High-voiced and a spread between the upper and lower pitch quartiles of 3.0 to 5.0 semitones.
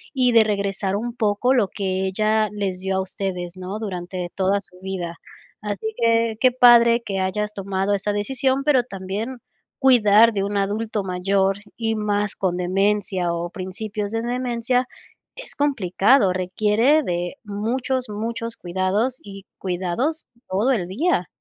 Yes: high, 205 Hz; average, 3.6 semitones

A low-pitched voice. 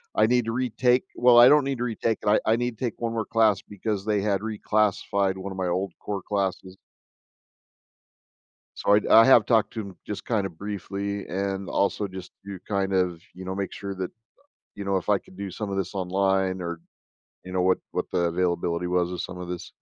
Yes: low, 100 Hz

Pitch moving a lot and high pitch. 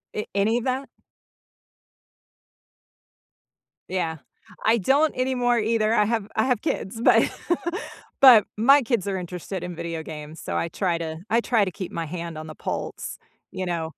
Yes: wide, 5.7 semitones; high, 200 Hz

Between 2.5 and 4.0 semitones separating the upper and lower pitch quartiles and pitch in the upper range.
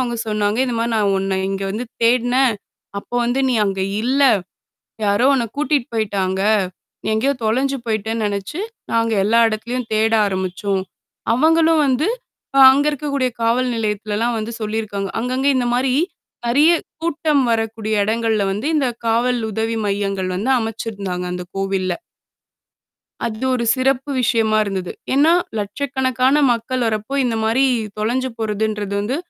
Yes: average, 3.7 semitones; high, 225 Hz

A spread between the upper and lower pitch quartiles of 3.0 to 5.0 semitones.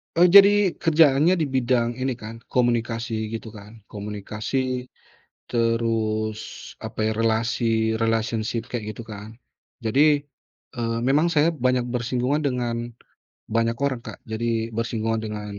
No: narrow, 2.5 semitones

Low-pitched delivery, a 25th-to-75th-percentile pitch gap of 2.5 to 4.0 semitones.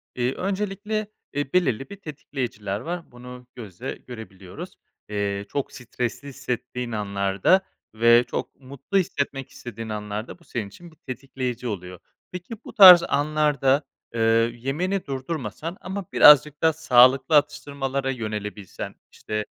No: low, 130 Hz; wide, 5.5 semitones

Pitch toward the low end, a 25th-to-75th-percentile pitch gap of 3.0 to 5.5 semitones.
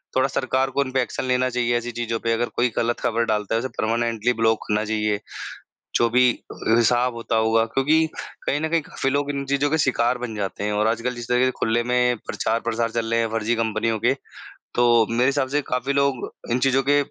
No: low, 120 Hz; narrow, 2.5 semitones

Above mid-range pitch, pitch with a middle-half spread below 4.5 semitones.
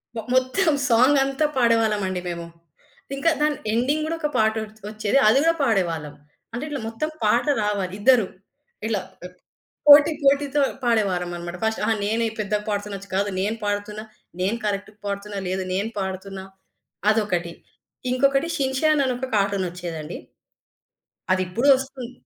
No: high, 215 Hz; average, 5.2 semitones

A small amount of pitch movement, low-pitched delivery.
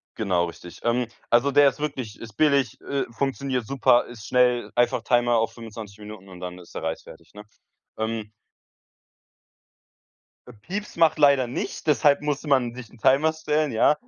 No: average, 4.2 semitones; low, 120 Hz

